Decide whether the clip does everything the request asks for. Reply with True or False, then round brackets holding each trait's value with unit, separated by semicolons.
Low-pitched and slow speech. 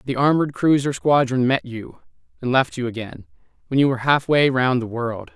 False (130 Hz; 200 wpm)